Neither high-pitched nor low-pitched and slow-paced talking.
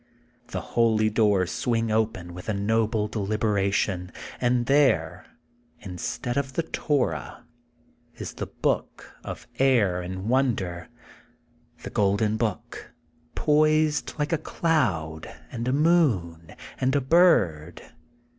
No: low, 115 Hz; slow, 115 wpm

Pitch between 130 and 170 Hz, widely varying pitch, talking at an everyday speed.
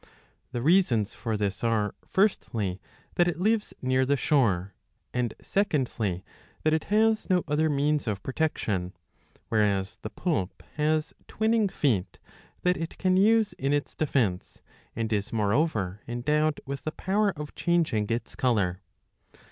Yes: low, 135 Hz; wide, 7.7 semitones; average, 145 wpm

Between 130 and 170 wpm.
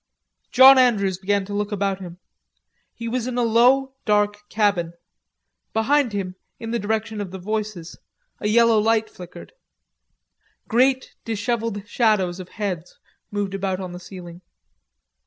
Yes: average, 140 wpm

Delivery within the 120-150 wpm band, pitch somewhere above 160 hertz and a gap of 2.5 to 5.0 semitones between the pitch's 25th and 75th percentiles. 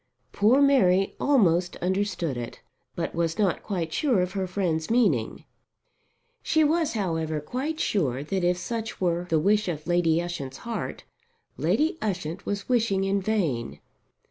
Yes: average, 145 wpm; medium, 185 Hz; average, 4.7 semitones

